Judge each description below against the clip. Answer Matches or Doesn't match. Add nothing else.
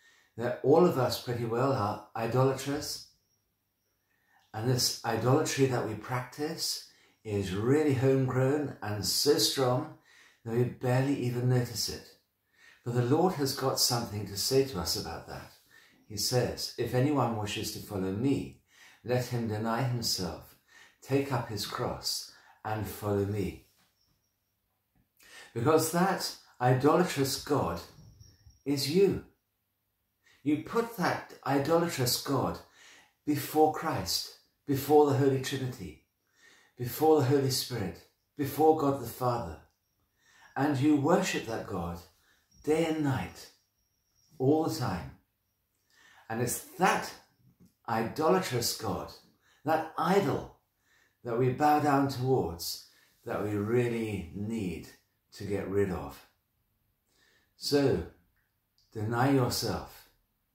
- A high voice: Doesn't match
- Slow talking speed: Matches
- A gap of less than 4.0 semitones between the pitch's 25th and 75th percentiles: Doesn't match